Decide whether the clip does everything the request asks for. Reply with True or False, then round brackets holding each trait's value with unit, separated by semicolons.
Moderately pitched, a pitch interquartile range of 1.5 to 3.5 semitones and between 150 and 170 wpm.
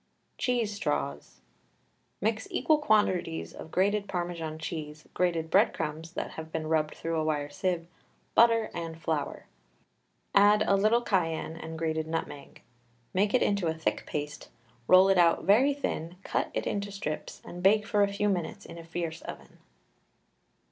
False (170 Hz; 4.2 semitones; 160 wpm)